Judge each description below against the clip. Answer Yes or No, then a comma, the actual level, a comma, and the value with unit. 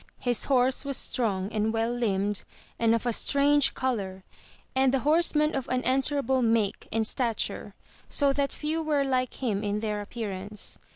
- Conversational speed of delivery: Yes, average, 170 wpm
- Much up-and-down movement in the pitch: No, average, 4.3 semitones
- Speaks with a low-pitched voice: No, high, 245 Hz